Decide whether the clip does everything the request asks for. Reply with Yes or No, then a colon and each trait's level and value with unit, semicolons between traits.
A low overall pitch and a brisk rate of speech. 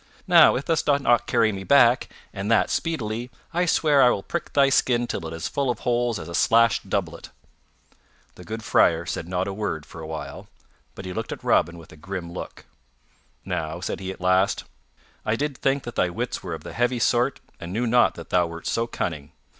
Yes: low, 110 Hz; fast, 220 wpm